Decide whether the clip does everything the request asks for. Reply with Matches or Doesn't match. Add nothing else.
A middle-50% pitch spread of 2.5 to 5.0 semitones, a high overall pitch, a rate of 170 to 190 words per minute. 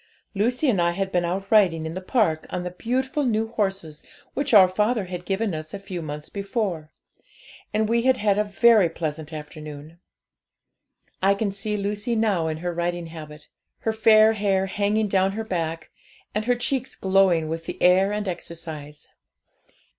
Matches